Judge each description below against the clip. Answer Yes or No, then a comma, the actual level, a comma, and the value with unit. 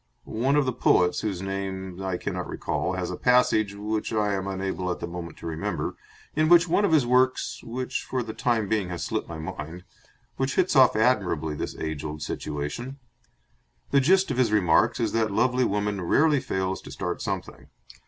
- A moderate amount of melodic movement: No, wide, 6.1 semitones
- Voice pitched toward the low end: Yes, low, 105 Hz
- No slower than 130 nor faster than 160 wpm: No, average, 190 wpm